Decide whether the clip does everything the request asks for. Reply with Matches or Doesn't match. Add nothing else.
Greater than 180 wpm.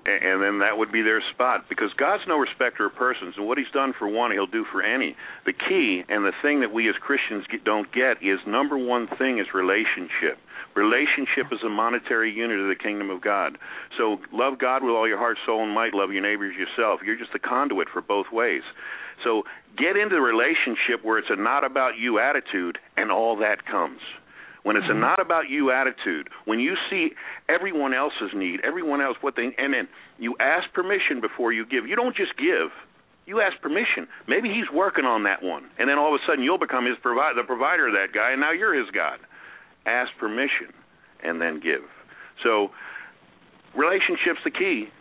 Matches